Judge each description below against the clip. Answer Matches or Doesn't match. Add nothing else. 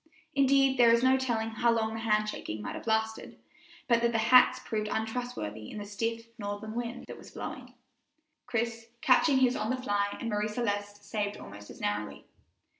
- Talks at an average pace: Matches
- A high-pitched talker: Matches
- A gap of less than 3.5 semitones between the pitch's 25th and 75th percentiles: Matches